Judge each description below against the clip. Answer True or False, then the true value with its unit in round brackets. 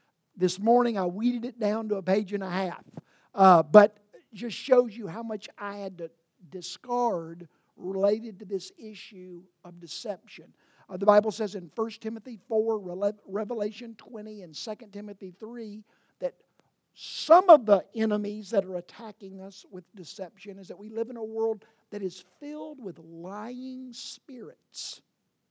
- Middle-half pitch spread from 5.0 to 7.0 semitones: False (3.0 semitones)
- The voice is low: False (210 Hz)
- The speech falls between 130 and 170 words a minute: True (160 wpm)